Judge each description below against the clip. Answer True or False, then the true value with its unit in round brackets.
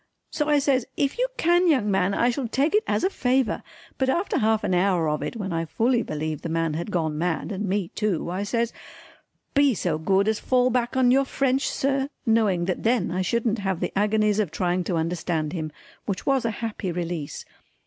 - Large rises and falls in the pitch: True (6.3 semitones)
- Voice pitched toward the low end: False (210 Hz)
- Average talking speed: False (215 wpm)